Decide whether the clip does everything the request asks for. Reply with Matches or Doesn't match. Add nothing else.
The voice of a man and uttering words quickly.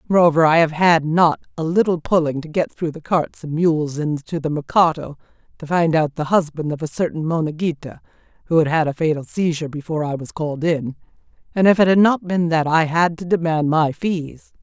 Doesn't match